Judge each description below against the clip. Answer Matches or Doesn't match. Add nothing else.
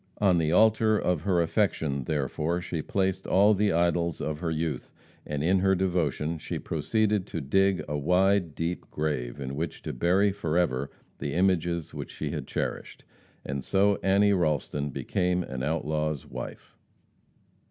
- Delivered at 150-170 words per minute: Matches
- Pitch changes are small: Doesn't match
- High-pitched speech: Doesn't match